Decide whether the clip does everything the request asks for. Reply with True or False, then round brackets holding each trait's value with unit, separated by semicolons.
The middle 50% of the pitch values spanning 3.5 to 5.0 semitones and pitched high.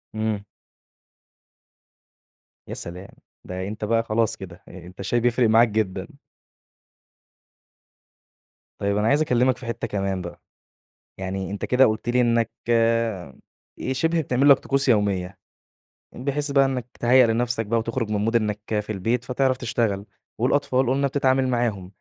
False (3.8 semitones; 115 Hz)